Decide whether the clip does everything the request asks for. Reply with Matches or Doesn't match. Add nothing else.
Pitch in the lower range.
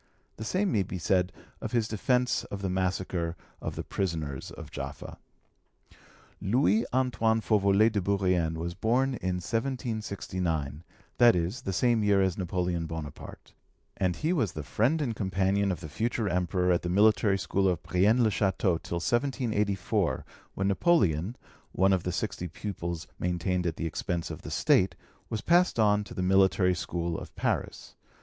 Matches